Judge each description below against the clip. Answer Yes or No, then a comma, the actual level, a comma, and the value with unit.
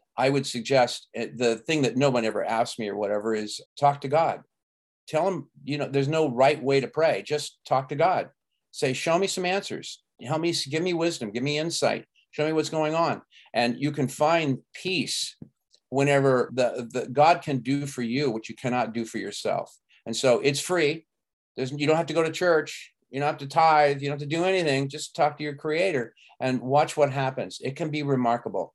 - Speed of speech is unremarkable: No, fast, 215 wpm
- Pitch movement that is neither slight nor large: Yes, average, 3.4 semitones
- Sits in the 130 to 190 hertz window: Yes, medium, 140 Hz